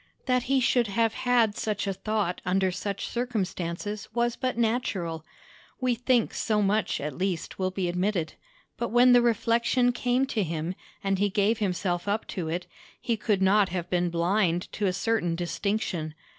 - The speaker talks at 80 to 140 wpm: No, average, 170 wpm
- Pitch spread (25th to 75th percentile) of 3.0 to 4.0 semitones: No, average, 4.5 semitones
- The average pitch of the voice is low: No, high, 205 Hz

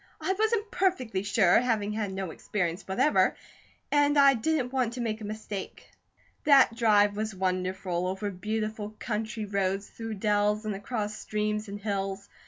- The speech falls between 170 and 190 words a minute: No, average, 155 wpm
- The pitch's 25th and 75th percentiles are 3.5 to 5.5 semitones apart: No, average, 2.7 semitones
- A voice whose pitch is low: No, high, 210 Hz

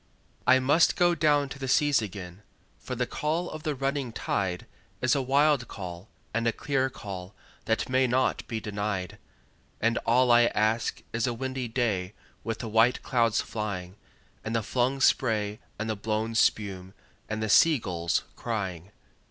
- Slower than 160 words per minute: No, average, 170 wpm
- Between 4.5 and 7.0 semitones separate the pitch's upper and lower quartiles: No, average, 4.0 semitones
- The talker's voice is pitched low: Yes, low, 115 Hz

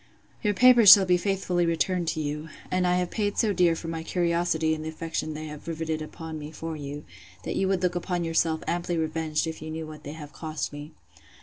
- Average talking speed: No, fast, 220 wpm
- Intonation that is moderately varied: No, narrow, 2.3 semitones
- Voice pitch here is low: No, medium, 165 Hz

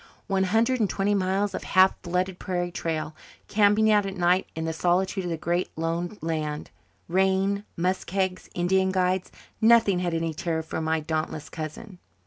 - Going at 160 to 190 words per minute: Yes, average, 165 wpm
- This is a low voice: No, medium, 185 Hz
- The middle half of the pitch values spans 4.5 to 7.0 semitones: No, average, 2.9 semitones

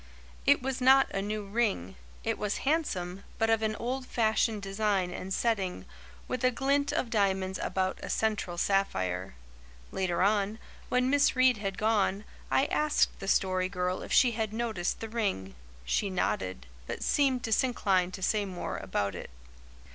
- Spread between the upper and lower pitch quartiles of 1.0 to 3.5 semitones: No, average, 4.2 semitones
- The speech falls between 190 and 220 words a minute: No, average, 160 wpm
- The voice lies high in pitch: Yes, high, 205 Hz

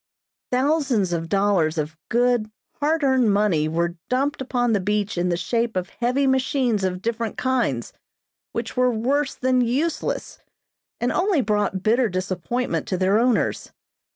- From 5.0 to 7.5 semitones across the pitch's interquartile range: Yes, average, 5.3 semitones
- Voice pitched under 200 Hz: No, high, 230 Hz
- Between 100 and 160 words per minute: Yes, average, 150 wpm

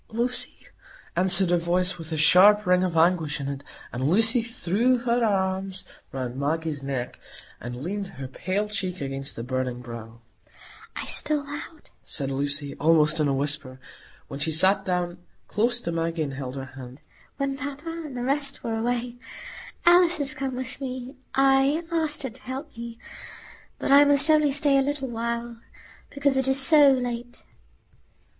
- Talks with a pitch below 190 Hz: No, high, 205 Hz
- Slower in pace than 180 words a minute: Yes, average, 170 wpm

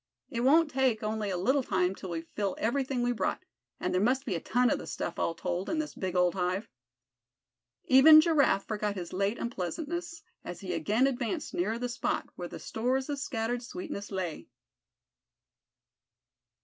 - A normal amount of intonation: No, wide, 6.0 semitones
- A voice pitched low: No, high, 230 Hz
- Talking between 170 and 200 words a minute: Yes, average, 175 wpm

